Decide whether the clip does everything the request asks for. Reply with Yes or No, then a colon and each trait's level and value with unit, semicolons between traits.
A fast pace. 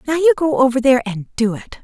Yes: fast, 260 wpm